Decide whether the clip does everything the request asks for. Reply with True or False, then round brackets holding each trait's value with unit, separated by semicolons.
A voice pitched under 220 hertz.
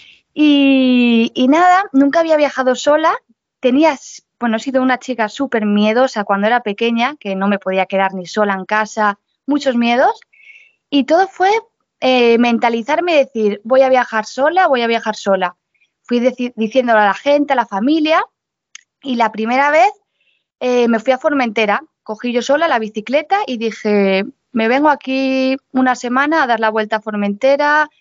False (255 Hz)